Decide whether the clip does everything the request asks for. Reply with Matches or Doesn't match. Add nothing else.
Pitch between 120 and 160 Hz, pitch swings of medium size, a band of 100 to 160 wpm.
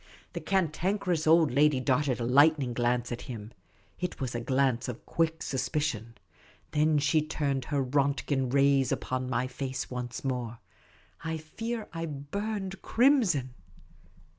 Matches